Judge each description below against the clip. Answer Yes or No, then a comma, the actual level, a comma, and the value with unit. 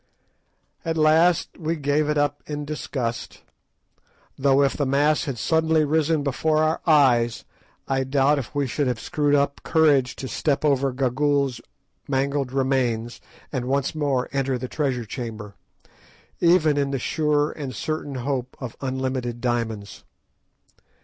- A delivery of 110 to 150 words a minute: Yes, average, 145 wpm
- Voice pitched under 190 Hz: Yes, medium, 140 Hz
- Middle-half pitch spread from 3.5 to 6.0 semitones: No, average, 2.7 semitones